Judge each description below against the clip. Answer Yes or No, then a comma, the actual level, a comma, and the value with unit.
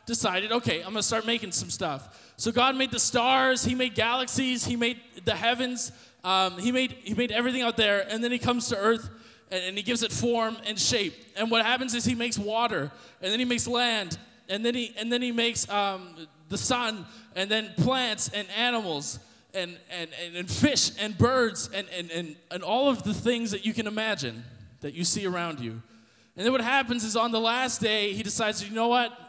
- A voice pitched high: Yes, high, 225 Hz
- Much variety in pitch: No, average, 4.2 semitones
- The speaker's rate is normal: No, fast, 220 wpm